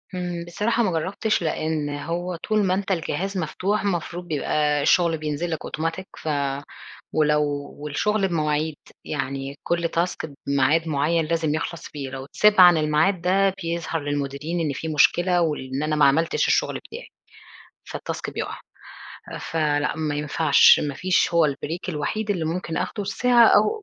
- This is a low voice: No, medium, 165 Hz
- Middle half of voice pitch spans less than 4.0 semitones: Yes, average, 3.3 semitones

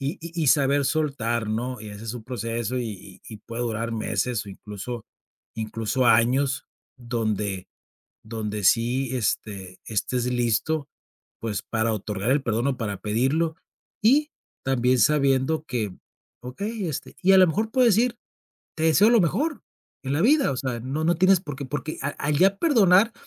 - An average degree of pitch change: No, wide, 5.9 semitones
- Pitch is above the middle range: No, low, 130 Hz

